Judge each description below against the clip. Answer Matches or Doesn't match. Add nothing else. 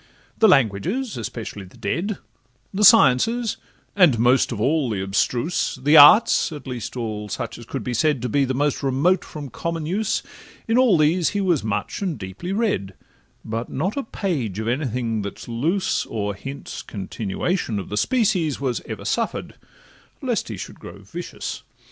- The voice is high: Doesn't match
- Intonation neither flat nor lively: Doesn't match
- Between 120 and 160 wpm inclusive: Doesn't match